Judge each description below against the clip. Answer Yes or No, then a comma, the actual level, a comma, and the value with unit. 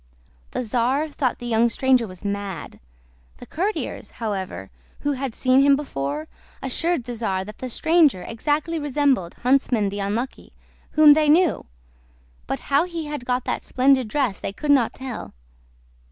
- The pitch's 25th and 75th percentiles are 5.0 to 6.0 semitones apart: Yes, wide, 5.4 semitones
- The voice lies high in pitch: Yes, very high, 255 Hz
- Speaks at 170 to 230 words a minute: No, average, 155 wpm